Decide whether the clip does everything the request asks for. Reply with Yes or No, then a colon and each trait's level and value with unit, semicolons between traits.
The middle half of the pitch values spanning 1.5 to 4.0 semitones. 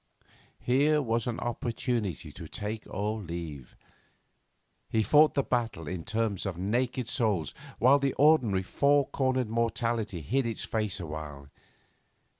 No: average, 5.1 semitones